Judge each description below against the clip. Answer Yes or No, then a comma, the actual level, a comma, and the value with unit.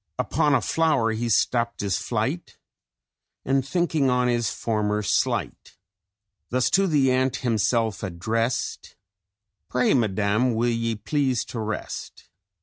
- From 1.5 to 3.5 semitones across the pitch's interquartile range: Yes, average, 3.1 semitones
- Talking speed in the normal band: No, slow, 125 wpm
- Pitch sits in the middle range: No, low, 120 Hz